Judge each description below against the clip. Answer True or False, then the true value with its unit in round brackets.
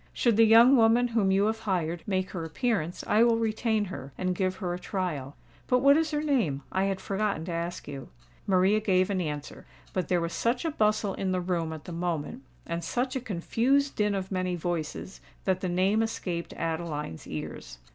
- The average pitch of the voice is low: False (190 Hz)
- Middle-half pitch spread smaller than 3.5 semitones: False (4.7 semitones)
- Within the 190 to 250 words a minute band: True (205 wpm)